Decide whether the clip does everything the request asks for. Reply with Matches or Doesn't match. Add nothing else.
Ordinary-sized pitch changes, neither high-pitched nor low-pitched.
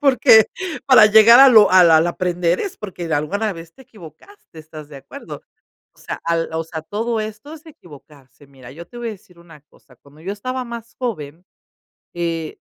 Doesn't match